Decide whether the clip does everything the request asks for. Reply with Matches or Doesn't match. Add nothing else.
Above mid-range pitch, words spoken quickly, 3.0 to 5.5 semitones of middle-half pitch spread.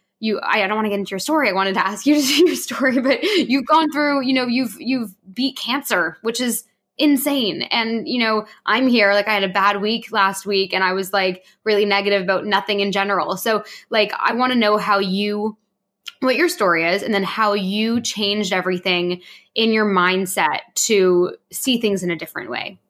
Matches